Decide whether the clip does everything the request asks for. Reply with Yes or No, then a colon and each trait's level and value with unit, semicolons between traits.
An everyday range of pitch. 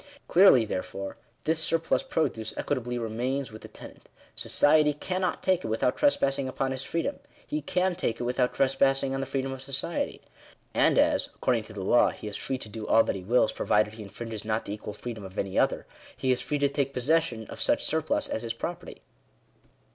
Yes: average, 4.6 semitones